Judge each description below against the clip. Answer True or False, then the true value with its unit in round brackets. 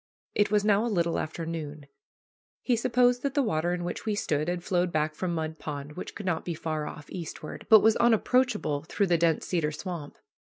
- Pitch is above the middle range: False (175 Hz)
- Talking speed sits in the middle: False (210 wpm)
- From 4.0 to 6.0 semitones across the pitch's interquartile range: True (5.1 semitones)